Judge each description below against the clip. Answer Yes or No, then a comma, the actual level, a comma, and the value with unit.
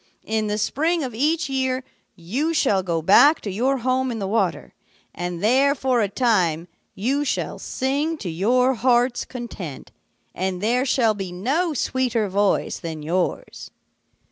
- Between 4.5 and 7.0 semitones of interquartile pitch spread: Yes, wide, 5.6 semitones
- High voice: Yes, high, 235 Hz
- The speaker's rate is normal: Yes, average, 155 wpm